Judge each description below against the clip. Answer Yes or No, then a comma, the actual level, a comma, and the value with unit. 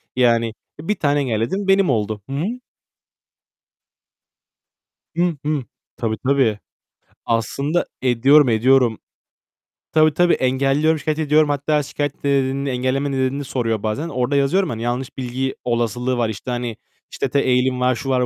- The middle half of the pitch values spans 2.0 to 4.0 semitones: Yes, average, 3.1 semitones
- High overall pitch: No, low, 130 Hz